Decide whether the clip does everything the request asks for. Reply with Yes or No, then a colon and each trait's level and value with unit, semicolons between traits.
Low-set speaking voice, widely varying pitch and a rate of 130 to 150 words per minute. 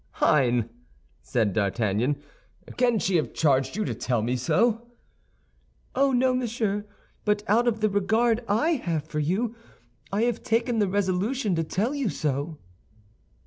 No: high, 205 Hz; wide, 8.0 semitones; average, 145 wpm